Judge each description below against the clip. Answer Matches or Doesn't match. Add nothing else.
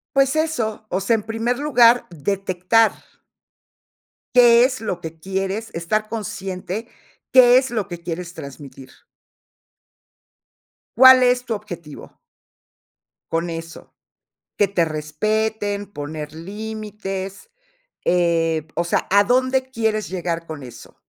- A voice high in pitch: Matches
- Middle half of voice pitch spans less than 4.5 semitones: Doesn't match